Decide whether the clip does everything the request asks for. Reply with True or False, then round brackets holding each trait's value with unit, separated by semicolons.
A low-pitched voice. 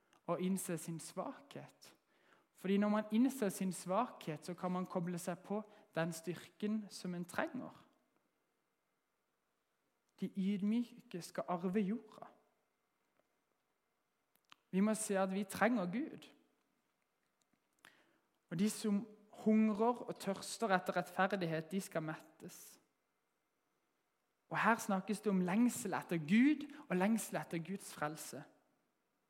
False (195 Hz)